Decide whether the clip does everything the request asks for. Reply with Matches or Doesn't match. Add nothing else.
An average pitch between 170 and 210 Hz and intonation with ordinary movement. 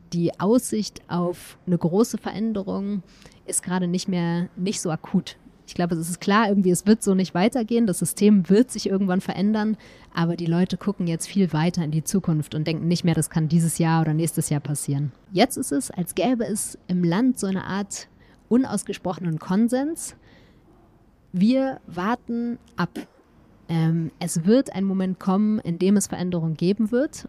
Matches